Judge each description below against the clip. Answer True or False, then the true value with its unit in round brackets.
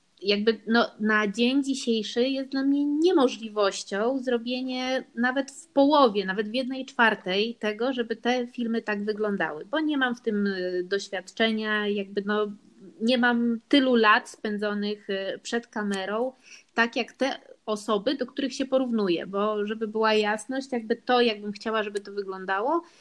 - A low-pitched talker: False (230 Hz)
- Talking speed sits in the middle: True (150 wpm)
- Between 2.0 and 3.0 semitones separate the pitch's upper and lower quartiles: False (3.5 semitones)